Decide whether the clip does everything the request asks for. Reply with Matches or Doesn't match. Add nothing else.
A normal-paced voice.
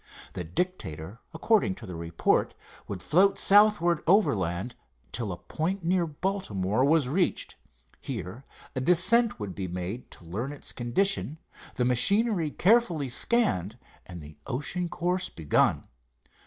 Doesn't match